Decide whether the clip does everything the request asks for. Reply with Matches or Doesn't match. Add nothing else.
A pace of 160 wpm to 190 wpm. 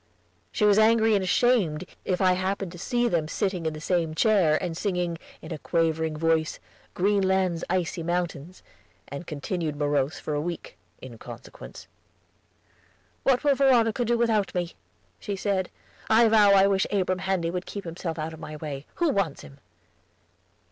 Matches